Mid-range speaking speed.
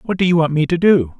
No: fast, 355 wpm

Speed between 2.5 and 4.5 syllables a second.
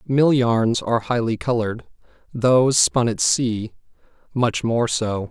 Yes: 4.1 syllables/s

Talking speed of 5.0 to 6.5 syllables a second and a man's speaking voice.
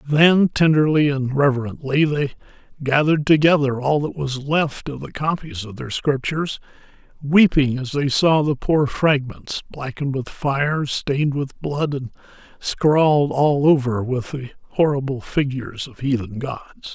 No: 4.4 syllables/s; male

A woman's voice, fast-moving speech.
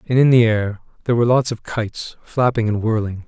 No: male; fast, 220 wpm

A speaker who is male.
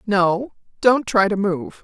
No: female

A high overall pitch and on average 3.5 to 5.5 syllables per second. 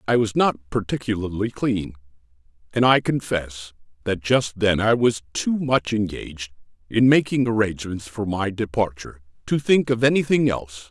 No: low, 110 Hz; 5.0 syllables/s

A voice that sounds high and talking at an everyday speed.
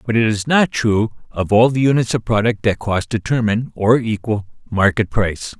No: low, 110 Hz; average, 195 wpm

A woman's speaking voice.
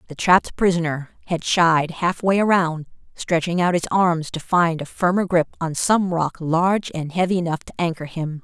Yes: female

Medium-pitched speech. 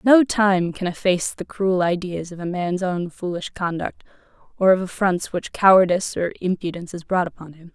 Yes: medium, 180 Hz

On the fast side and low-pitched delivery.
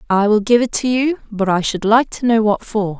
No: fast, 280 wpm; high, 220 Hz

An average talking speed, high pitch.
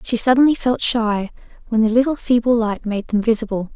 Yes: average, 190 wpm; high, 230 Hz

